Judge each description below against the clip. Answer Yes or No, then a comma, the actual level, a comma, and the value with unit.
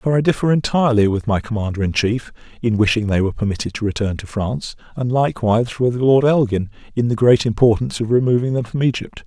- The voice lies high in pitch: No, low, 115 Hz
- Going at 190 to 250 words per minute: Yes, fast, 205 wpm